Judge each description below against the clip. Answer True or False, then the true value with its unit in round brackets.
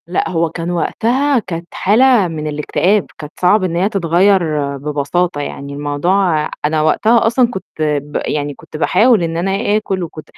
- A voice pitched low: False (170 Hz)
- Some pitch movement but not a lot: True (4.6 semitones)